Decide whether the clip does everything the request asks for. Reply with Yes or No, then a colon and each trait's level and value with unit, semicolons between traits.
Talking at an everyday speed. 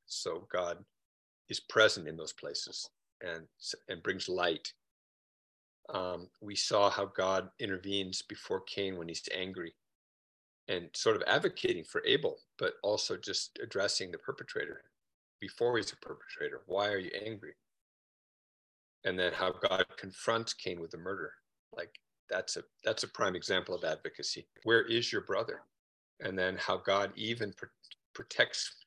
Yes: average, 150 wpm